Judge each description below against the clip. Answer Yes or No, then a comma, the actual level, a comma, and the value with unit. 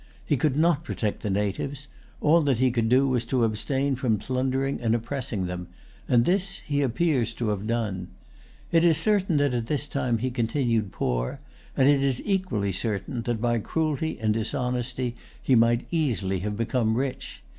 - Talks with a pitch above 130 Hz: No, low, 125 Hz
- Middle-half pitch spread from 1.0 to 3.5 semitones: No, average, 4.2 semitones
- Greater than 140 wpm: Yes, average, 175 wpm